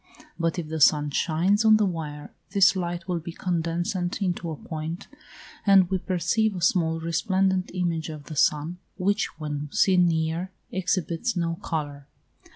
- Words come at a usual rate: Yes, average, 160 wpm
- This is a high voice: No, medium, 170 Hz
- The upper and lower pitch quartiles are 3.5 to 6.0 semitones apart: No, average, 2.7 semitones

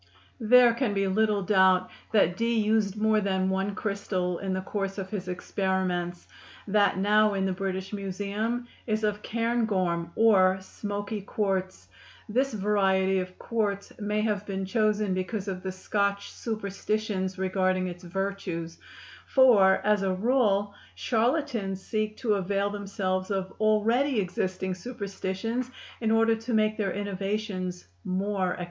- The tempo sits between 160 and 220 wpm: No, average, 140 wpm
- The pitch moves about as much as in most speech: No, narrow, 2.3 semitones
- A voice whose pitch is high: Yes, high, 200 Hz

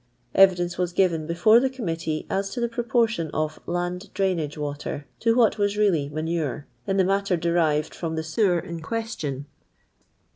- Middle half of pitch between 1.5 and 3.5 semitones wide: No, average, 4.3 semitones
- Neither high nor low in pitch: Yes, medium, 175 Hz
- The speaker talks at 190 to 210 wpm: No, average, 160 wpm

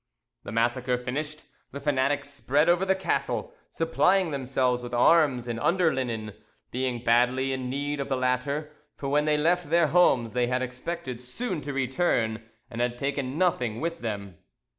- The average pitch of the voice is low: Yes, low, 130 Hz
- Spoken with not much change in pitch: No, average, 3.8 semitones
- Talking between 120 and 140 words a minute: No, average, 165 wpm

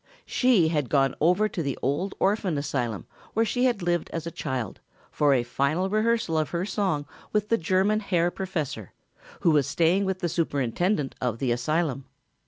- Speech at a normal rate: Yes, average, 180 wpm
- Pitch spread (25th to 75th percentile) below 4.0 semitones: No, wide, 5.6 semitones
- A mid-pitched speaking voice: Yes, medium, 165 Hz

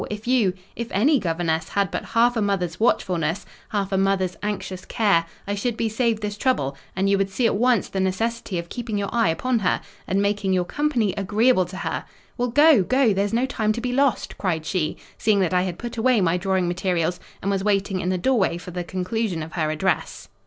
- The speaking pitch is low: No, high, 200 Hz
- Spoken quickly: Yes, fast, 210 wpm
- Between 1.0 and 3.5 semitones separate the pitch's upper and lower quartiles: No, average, 4.1 semitones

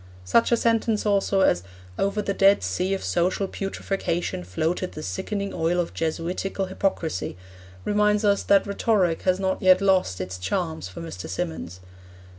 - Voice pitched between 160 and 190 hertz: Yes, medium, 185 Hz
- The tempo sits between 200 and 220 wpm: No, average, 155 wpm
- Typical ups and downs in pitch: Yes, average, 3.9 semitones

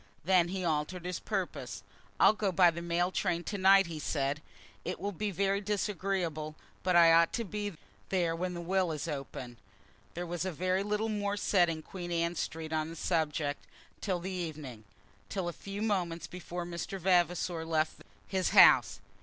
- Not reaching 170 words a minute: No, average, 180 wpm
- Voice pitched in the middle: Yes, medium, 175 Hz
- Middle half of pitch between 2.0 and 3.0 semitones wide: Yes, average, 2.7 semitones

